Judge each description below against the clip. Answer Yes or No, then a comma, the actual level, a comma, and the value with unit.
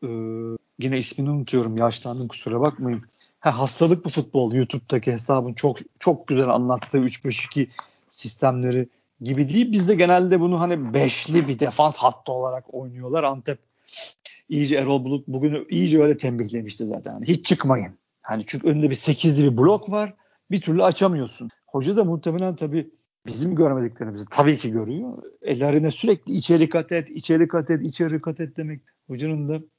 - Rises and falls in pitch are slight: No, average, 4.6 semitones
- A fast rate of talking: Yes, fast, 160 wpm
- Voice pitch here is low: No, medium, 145 Hz